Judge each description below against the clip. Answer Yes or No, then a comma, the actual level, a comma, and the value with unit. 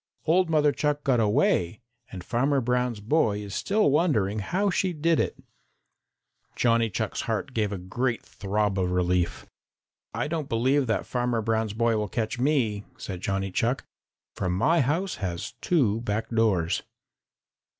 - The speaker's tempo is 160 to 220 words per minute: No, average, 150 wpm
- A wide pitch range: Yes, wide, 5.9 semitones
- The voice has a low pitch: Yes, low, 115 Hz